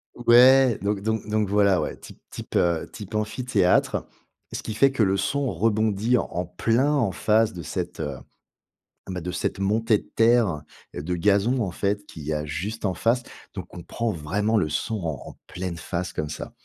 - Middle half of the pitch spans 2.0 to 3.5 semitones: No, average, 4.2 semitones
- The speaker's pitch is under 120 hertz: Yes, low, 100 Hz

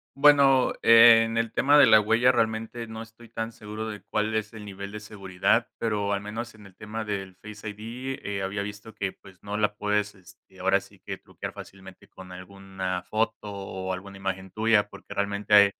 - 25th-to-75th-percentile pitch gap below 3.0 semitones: Yes, narrow, 2.4 semitones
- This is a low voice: Yes, low, 105 Hz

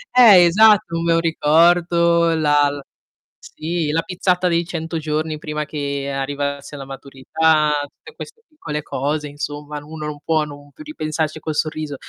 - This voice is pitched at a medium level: Yes, medium, 155 Hz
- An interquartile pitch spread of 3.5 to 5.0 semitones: No, narrow, 2.4 semitones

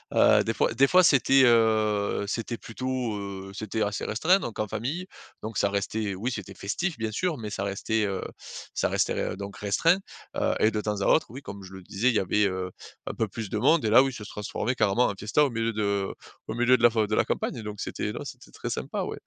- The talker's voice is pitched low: Yes, low, 110 Hz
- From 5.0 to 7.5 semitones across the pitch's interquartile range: No, average, 3.3 semitones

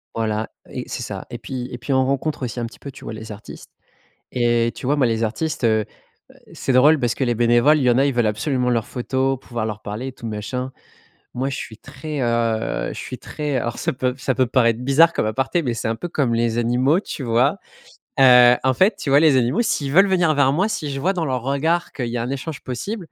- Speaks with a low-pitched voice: Yes, low, 130 Hz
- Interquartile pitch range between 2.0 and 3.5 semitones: Yes, average, 3.2 semitones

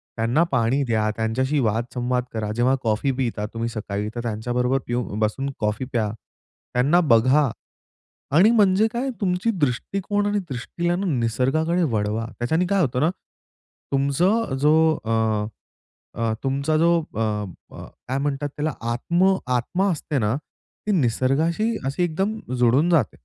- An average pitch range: No, wide, 6.5 semitones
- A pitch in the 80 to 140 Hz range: Yes, low, 135 Hz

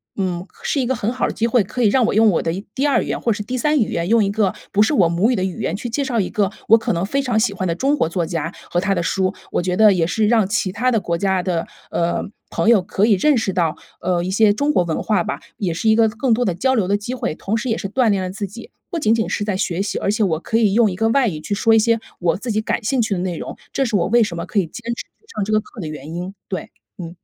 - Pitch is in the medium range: No, high, 205 Hz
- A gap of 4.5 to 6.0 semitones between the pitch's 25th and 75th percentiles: No, average, 4.1 semitones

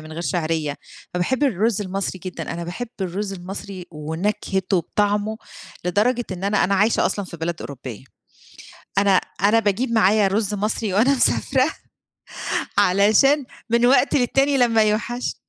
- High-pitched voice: Yes, high, 205 Hz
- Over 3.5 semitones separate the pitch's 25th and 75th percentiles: Yes, average, 4.1 semitones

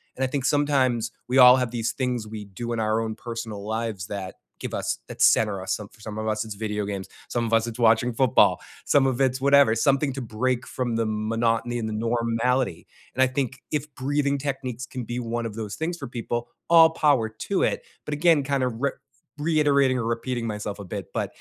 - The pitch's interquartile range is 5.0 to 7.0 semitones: No, average, 3.3 semitones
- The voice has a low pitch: Yes, low, 120 Hz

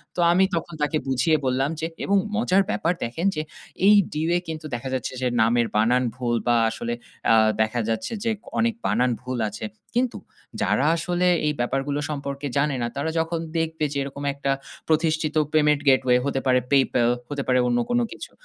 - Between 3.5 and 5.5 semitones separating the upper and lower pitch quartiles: Yes, average, 4.3 semitones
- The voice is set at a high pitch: No, medium, 140 Hz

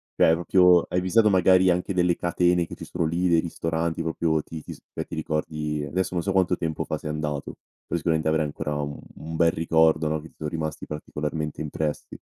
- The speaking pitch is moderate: No, very low, 80 Hz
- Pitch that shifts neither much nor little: No, narrow, 2.3 semitones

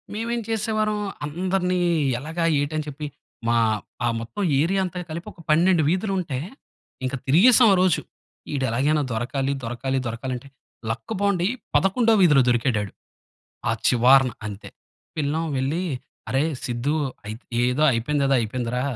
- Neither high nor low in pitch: Yes, medium, 145 Hz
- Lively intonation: Yes, wide, 6.3 semitones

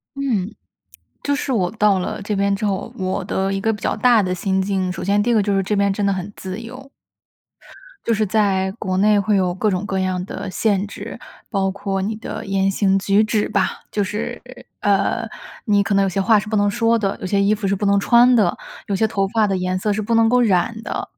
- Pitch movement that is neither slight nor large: No, narrow, 2.1 semitones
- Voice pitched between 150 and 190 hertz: No, high, 200 Hz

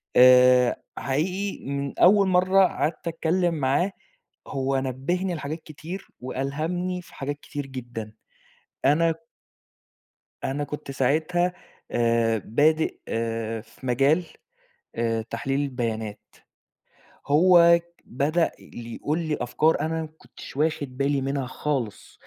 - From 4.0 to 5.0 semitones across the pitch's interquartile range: Yes, average, 4.7 semitones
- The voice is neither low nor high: Yes, medium, 145 Hz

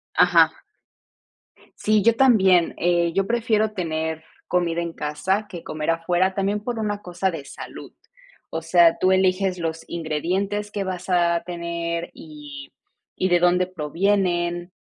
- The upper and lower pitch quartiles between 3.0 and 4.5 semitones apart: No, narrow, 2.6 semitones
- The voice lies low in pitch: No, medium, 175 Hz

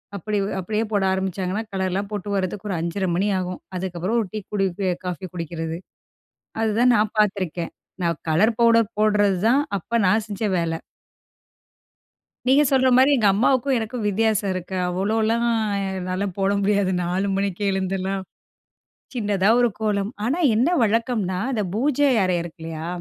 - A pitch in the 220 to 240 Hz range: No, high, 200 Hz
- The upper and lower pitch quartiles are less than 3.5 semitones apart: Yes, average, 3.1 semitones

